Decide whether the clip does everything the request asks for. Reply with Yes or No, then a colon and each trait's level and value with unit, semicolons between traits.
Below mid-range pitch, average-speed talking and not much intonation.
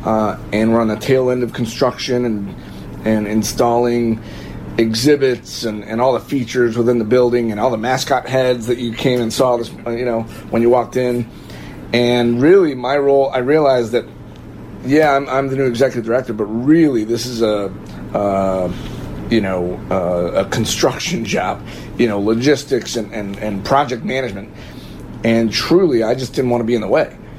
Yes: low, 120 Hz; average, 180 wpm; narrow, 2.3 semitones